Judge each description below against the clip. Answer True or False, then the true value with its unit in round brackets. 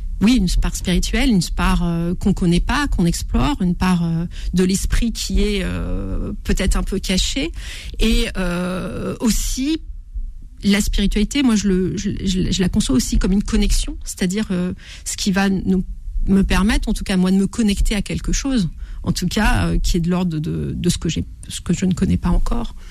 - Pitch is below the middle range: False (190 Hz)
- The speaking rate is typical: True (205 wpm)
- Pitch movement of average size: True (3.0 semitones)